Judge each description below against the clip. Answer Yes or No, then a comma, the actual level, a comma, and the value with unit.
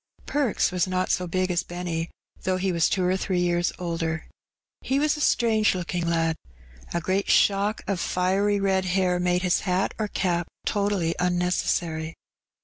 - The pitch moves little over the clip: Yes, narrow, 2.0 semitones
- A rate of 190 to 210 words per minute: No, average, 160 wpm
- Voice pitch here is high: No, medium, 180 Hz